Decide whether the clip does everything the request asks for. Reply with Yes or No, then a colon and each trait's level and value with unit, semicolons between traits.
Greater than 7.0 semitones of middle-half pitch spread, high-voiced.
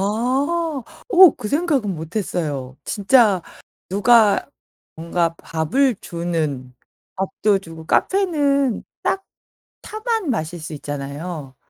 Yes: wide, 8.9 semitones; high, 195 Hz